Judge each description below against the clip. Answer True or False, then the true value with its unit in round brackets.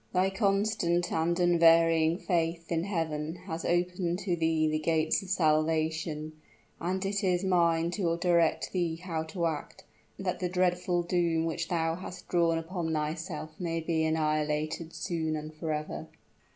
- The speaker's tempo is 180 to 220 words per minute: False (150 wpm)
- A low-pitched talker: False (165 Hz)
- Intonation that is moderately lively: False (1.8 semitones)